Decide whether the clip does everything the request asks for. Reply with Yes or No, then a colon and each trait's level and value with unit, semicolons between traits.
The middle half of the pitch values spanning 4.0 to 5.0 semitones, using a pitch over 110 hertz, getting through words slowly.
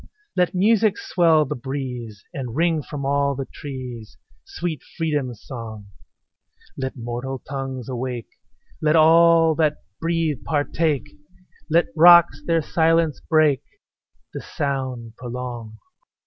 Yes: average, 4.5 semitones; medium, 140 Hz; slow, 115 wpm